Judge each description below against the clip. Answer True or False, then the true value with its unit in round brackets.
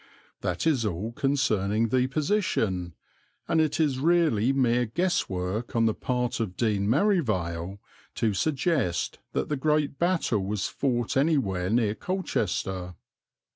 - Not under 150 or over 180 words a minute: False (135 wpm)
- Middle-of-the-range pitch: False (120 Hz)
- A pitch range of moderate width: False (7.1 semitones)